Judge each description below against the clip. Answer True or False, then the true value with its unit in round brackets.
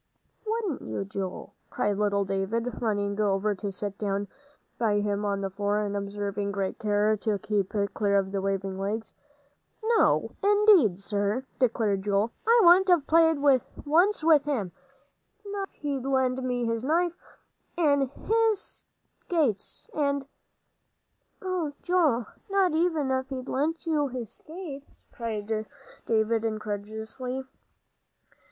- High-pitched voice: True (230 Hz)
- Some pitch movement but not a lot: False (7.0 semitones)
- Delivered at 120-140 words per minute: True (135 wpm)